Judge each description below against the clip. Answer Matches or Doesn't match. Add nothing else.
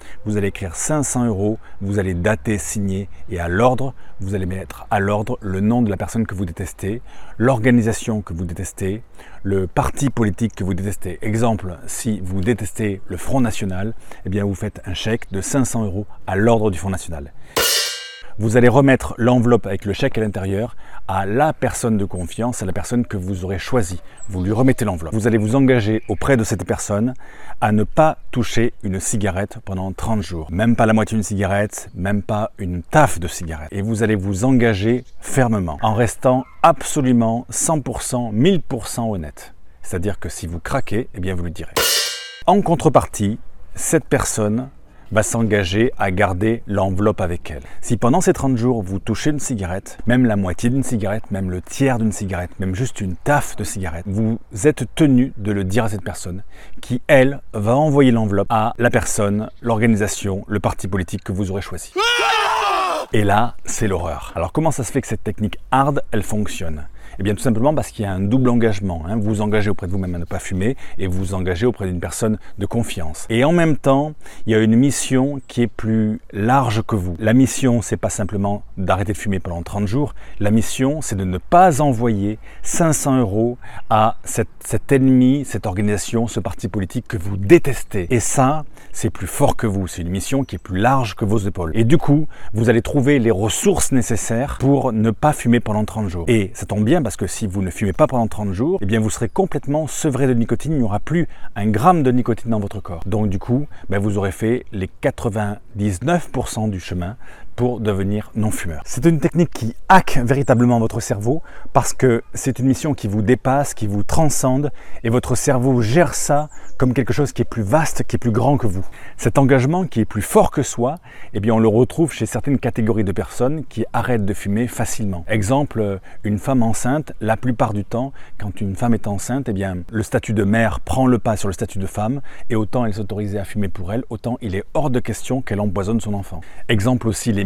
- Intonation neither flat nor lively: Matches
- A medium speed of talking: Matches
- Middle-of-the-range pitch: Doesn't match